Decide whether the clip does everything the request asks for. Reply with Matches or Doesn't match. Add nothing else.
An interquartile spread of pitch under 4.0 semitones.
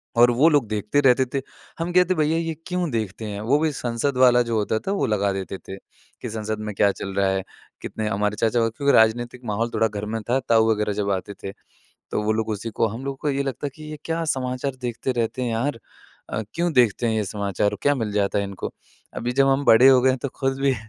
Doesn't match